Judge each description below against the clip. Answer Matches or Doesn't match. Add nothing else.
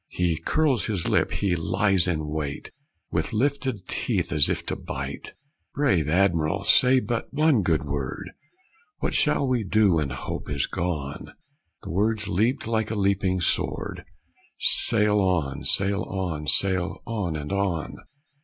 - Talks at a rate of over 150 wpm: Doesn't match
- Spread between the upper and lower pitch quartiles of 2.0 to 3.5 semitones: Doesn't match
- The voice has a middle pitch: Doesn't match